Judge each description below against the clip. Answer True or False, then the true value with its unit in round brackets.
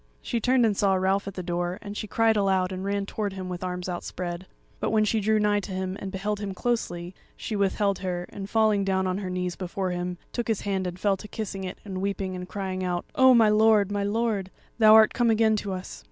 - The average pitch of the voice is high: True (195 Hz)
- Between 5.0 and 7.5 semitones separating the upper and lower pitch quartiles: False (2.4 semitones)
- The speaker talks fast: True (240 wpm)